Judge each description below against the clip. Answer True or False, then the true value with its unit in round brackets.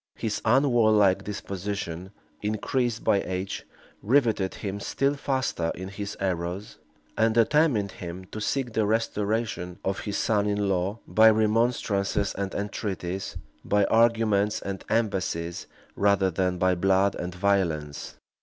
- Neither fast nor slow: False (125 wpm)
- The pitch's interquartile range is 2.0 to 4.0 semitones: True (2.8 semitones)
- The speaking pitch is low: True (100 Hz)